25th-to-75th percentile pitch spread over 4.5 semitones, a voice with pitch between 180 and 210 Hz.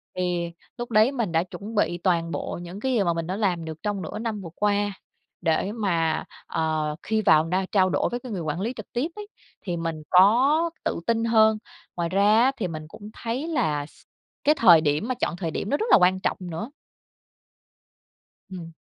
Yes: average, 5.1 semitones; high, 190 Hz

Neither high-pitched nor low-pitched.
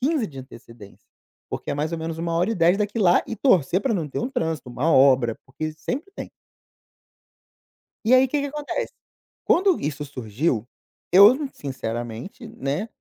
Yes: medium, 165 Hz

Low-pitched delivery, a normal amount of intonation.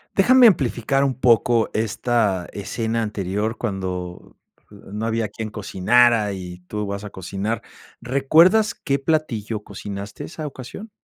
Yes: low, 110 Hz; average, 4.6 semitones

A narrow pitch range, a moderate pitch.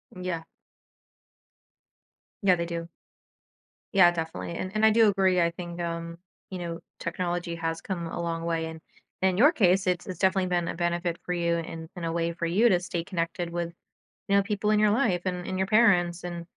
Yes: narrow, 1.9 semitones; medium, 175 Hz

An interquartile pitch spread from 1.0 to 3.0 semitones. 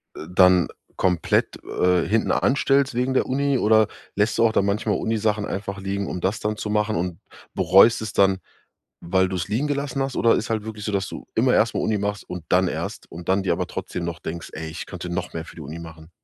No: average, 3.5 semitones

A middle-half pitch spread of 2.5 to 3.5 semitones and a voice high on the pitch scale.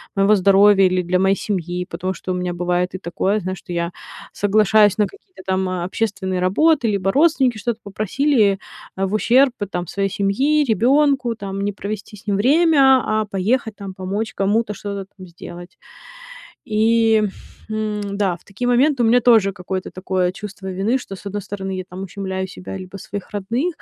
Yes: average, 3.2 semitones; high, 200 Hz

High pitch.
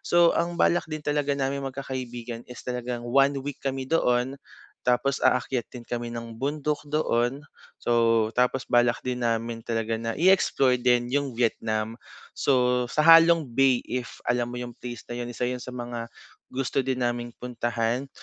No: low, 125 Hz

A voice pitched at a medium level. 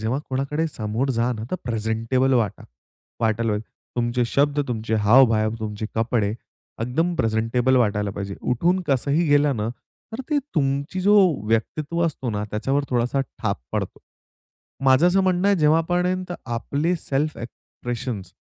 No: low, 125 Hz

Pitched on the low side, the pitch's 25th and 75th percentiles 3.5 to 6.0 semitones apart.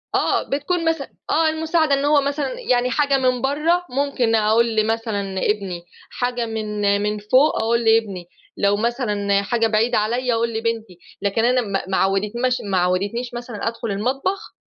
No: high, 230 Hz; average, 4.3 semitones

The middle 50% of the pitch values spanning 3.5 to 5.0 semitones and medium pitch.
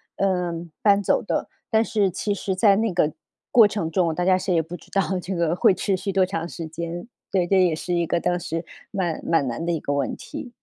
No: average, 2.8 semitones; medium, 180 Hz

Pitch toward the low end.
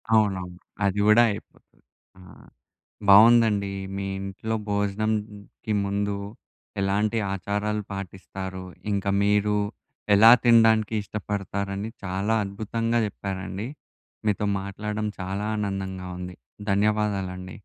Yes: low, 100 Hz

